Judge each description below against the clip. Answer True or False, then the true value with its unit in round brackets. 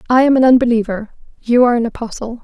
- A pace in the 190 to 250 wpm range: True (200 wpm)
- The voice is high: True (240 Hz)